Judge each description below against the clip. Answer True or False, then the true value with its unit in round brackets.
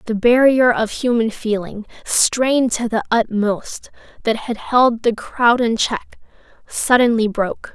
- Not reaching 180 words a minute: True (140 wpm)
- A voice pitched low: False (230 Hz)